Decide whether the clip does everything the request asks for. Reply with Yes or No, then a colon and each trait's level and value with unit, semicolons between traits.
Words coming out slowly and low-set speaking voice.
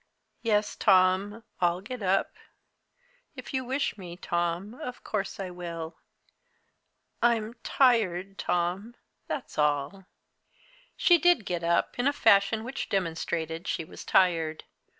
No: slow, 125 wpm; high, 195 Hz